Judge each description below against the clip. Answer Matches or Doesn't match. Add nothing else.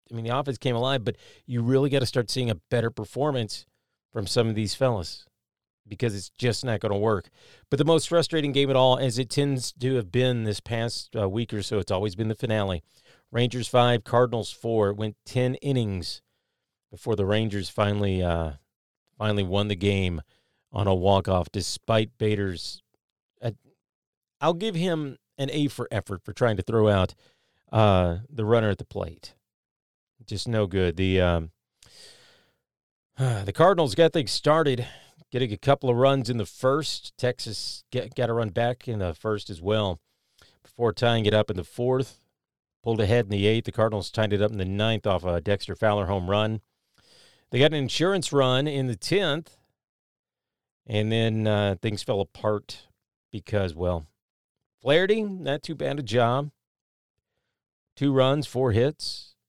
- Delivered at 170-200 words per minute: Matches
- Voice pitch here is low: Matches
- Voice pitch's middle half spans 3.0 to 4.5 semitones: Matches